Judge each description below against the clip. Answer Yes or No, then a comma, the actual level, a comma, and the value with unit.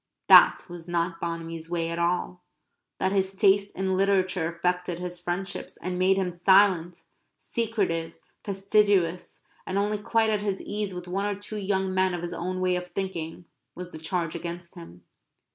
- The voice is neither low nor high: Yes, medium, 180 Hz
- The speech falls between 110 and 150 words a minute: No, average, 170 wpm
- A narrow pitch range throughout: Yes, narrow, 2.2 semitones